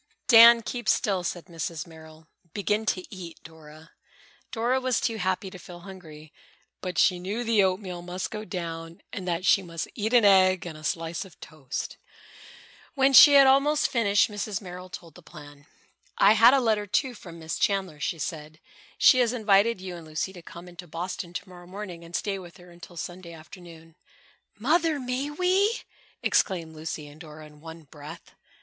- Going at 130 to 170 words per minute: No, average, 180 wpm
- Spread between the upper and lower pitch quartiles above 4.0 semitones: Yes, average, 4.7 semitones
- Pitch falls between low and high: Yes, medium, 180 Hz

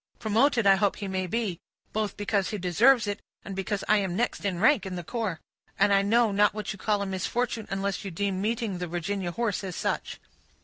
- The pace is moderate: No, fast, 220 wpm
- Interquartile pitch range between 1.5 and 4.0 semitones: Yes, narrow, 2.4 semitones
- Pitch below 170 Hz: No, high, 200 Hz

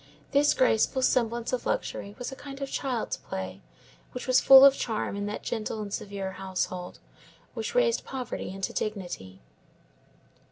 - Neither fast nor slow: Yes, average, 155 wpm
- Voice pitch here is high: Yes, high, 225 Hz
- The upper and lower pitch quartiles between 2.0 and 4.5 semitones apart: No, wide, 5.4 semitones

